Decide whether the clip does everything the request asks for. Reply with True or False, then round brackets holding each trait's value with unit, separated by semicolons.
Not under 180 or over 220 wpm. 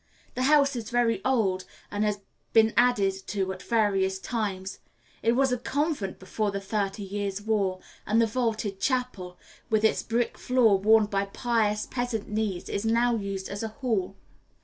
False (170 wpm)